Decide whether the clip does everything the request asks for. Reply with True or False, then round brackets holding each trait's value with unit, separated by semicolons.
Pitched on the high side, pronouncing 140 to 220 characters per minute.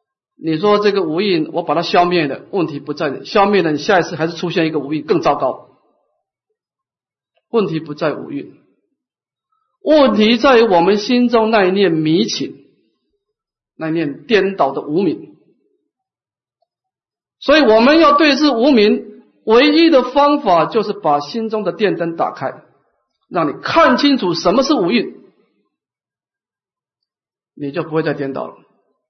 True (210 Hz; 215 characters per minute)